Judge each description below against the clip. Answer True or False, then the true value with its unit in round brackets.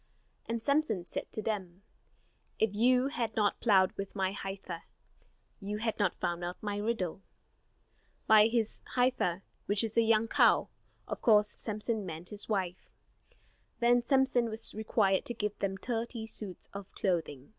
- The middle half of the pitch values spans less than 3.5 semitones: True (3.0 semitones)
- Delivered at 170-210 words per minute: False (155 wpm)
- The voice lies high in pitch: True (210 Hz)